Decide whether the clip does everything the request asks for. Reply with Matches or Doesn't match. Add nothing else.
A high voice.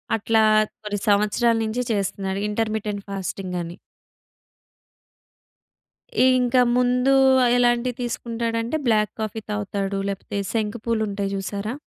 Matches